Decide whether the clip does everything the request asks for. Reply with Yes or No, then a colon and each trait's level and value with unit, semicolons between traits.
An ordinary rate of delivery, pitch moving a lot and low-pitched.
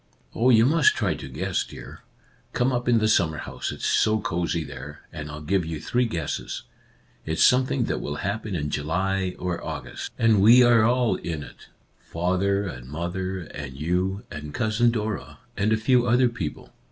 Yes: average, 185 wpm; wide, 6.3 semitones; very low, 95 Hz